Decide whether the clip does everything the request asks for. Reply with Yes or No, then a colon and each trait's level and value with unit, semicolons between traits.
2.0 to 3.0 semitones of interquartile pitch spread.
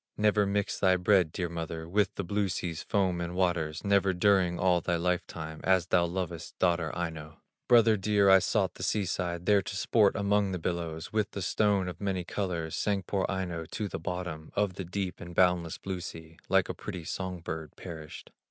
Yes: average, 2.7 semitones